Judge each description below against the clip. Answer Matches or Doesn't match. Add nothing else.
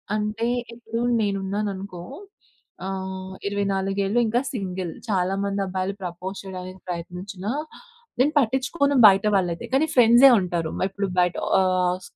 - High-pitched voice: Matches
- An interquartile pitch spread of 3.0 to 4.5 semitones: Doesn't match